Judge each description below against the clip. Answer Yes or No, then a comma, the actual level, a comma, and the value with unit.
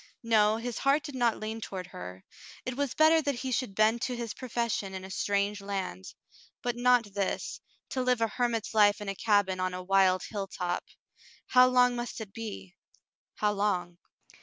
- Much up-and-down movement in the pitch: No, average, 4.0 semitones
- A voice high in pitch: Yes, high, 215 Hz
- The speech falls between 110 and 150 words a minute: No, average, 185 wpm